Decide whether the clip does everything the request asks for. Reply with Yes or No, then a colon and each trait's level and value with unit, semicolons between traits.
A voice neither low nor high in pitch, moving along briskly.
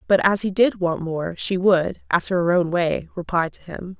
Yes: medium, 180 Hz; fast, 225 wpm